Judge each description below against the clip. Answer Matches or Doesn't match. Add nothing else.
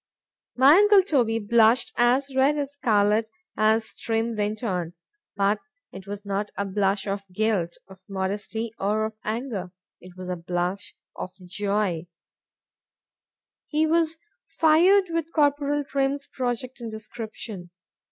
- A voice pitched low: Doesn't match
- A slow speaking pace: Matches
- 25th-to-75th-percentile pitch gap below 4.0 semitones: Doesn't match